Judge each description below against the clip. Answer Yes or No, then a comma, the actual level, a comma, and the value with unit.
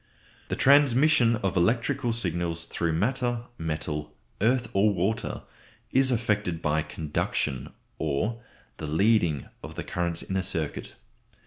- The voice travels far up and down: Yes, wide, 6.3 semitones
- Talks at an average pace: No, slow, 130 wpm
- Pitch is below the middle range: Yes, very low, 95 Hz